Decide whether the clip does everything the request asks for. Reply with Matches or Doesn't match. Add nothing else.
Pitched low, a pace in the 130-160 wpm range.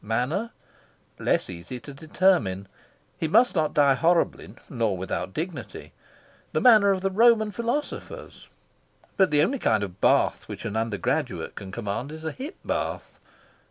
Doesn't match